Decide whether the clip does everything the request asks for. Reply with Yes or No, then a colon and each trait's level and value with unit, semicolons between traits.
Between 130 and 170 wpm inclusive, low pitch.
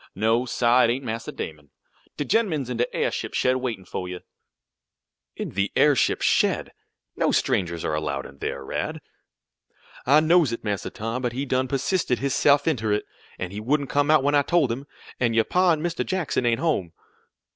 No: average, 190 wpm; low, 125 Hz